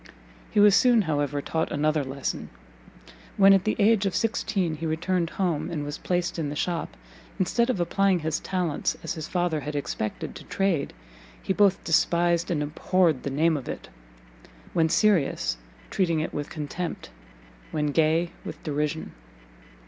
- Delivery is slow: No, average, 160 wpm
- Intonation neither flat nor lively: Yes, average, 3.8 semitones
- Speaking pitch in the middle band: Yes, medium, 165 Hz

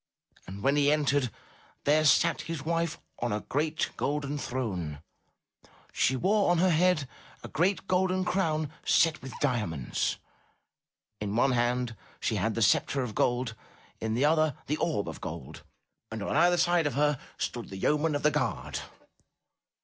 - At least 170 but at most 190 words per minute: No, average, 160 wpm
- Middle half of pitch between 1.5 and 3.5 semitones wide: No, average, 5.0 semitones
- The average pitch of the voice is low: No, medium, 145 Hz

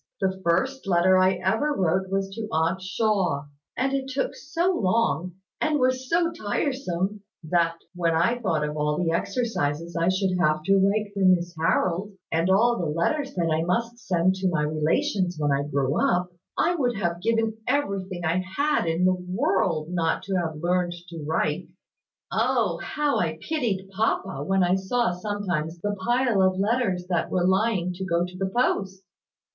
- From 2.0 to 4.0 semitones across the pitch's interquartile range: No, average, 4.4 semitones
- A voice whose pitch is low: No, medium, 185 Hz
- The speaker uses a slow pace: No, average, 175 wpm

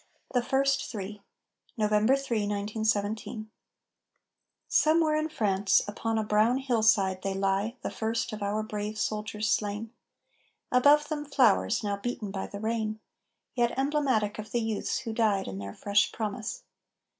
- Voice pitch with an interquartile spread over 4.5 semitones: No, average, 2.9 semitones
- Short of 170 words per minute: Yes, average, 145 wpm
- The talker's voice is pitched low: No, high, 215 Hz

